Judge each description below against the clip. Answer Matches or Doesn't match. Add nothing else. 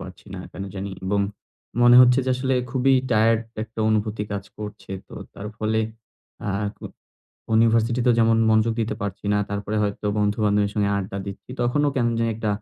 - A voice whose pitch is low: Matches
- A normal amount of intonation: Doesn't match